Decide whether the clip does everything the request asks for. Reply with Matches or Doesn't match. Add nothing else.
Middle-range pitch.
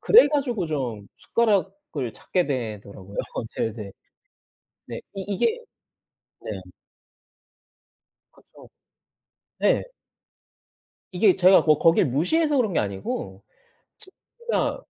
Matches